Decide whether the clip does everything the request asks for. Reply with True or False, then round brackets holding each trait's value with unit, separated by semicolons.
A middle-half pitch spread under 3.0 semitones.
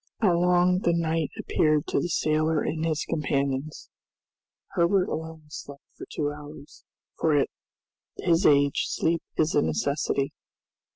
True (2.6 semitones)